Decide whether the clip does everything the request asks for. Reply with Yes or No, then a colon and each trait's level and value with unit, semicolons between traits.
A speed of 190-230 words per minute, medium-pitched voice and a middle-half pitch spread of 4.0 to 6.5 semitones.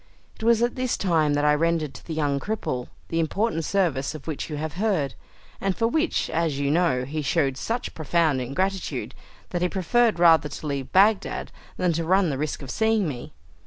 Yes: average, 200 wpm; medium, 165 Hz; average, 5.0 semitones